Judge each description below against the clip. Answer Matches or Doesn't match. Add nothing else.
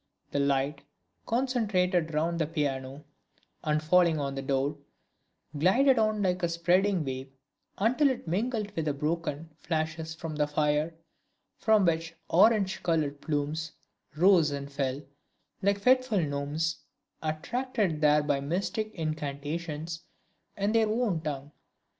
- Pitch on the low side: Doesn't match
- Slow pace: Matches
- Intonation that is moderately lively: Matches